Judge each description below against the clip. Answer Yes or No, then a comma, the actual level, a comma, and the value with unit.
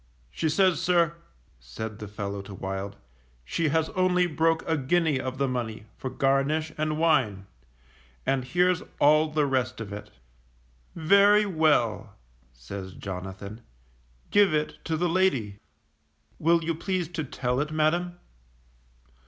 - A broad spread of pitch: Yes, wide, 7.3 semitones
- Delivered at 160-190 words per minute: No, slow, 135 wpm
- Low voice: No, medium, 150 Hz